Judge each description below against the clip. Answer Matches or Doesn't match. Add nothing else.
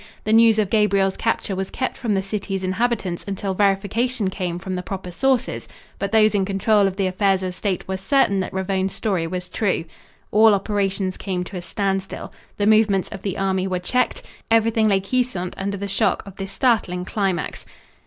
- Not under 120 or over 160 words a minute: Doesn't match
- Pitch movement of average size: Doesn't match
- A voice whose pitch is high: Matches